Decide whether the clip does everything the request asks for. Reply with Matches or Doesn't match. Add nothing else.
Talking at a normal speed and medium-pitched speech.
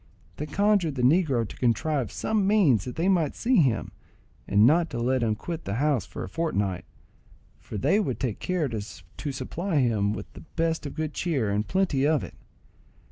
Matches